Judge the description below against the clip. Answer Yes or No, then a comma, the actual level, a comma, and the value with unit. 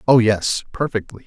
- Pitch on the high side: No, low, 115 Hz